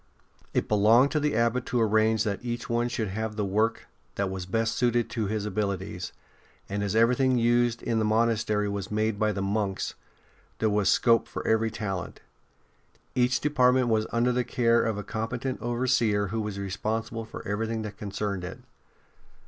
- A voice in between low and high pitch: No, low, 110 Hz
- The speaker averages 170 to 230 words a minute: Yes, average, 175 wpm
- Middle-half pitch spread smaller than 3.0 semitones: Yes, narrow, 2.4 semitones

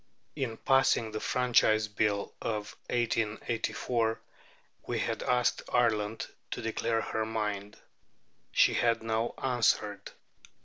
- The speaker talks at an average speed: No, slow, 105 wpm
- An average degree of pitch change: No, narrow, 1.9 semitones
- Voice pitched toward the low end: Yes, low, 110 Hz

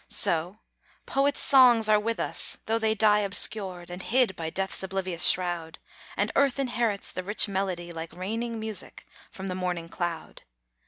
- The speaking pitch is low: No, high, 195 Hz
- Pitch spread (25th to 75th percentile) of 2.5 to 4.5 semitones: Yes, average, 4.0 semitones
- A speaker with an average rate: Yes, average, 160 wpm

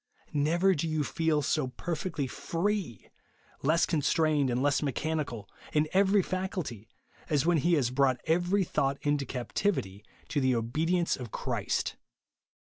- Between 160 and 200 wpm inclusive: No, average, 150 wpm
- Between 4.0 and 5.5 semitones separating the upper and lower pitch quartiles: Yes, average, 4.4 semitones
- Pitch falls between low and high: Yes, medium, 155 Hz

